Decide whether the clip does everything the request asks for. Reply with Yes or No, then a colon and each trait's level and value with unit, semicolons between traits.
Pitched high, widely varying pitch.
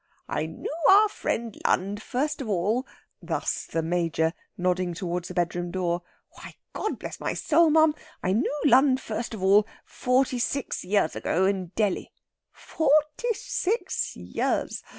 Yes: high, 210 Hz; wide, 8.0 semitones